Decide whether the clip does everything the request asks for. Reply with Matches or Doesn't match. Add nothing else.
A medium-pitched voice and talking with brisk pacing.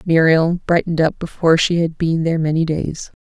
Doesn't match